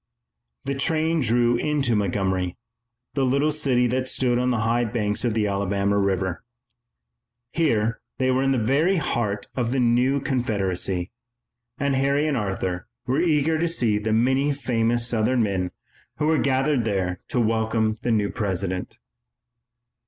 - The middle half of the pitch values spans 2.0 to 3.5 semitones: No, average, 4.6 semitones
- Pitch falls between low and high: No, low, 120 Hz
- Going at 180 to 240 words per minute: No, average, 150 wpm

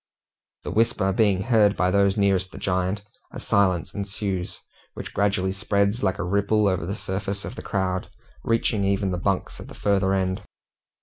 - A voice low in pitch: Yes, low, 100 Hz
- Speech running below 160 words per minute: No, average, 175 wpm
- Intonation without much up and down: Yes, narrow, 1.5 semitones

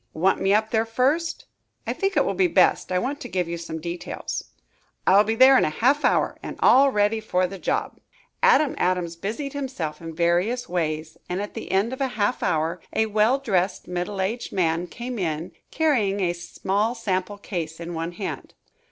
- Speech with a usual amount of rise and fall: No, wide, 5.8 semitones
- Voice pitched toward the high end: Yes, high, 195 Hz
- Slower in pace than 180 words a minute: No, average, 195 wpm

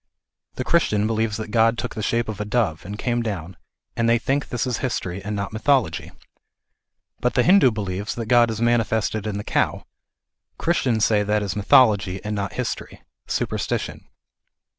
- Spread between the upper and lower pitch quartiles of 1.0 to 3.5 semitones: Yes, narrow, 2.5 semitones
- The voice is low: Yes, low, 110 Hz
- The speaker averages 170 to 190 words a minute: Yes, average, 180 wpm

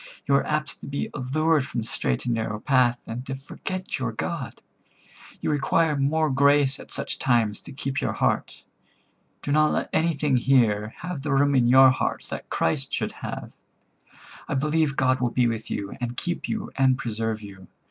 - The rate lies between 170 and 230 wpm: Yes, average, 190 wpm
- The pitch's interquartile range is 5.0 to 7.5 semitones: No, average, 3.7 semitones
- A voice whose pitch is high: No, low, 135 Hz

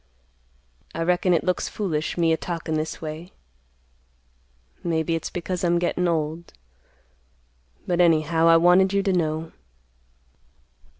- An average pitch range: No, narrow, 1.8 semitones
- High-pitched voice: No, medium, 170 Hz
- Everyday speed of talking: No, slow, 125 wpm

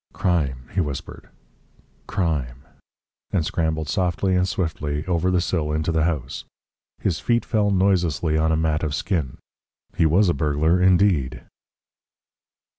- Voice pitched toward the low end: Yes, very low, 80 Hz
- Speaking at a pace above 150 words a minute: No, slow, 135 wpm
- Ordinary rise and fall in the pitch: Yes, average, 3.4 semitones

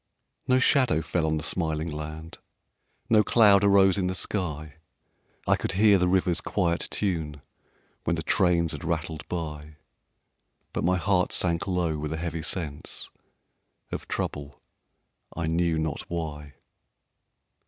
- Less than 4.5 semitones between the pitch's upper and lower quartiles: Yes, average, 2.9 semitones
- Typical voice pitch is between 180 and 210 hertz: No, very low, 85 Hz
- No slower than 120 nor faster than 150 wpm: Yes, average, 140 wpm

